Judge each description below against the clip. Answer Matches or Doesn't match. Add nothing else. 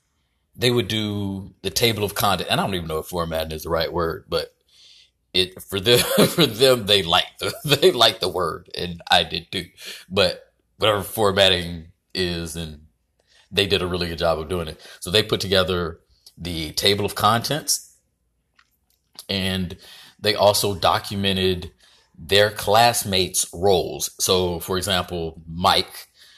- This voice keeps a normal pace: Matches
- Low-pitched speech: Matches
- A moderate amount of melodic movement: Matches